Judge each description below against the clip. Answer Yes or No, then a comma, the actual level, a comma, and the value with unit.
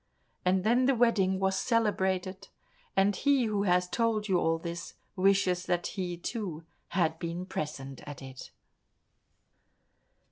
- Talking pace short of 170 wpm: Yes, slow, 135 wpm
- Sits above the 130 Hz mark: Yes, high, 190 Hz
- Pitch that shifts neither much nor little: Yes, average, 3.2 semitones